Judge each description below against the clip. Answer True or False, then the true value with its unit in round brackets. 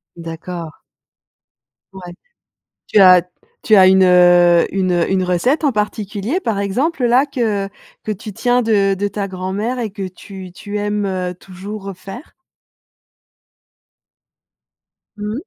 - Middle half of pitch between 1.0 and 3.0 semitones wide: True (2.7 semitones)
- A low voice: False (195 Hz)